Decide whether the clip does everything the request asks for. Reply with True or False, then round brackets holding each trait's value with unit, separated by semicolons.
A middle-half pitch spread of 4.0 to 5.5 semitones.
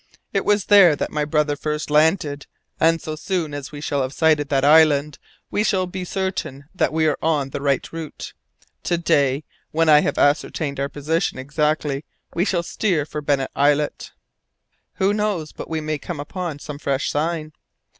False (2.5 semitones)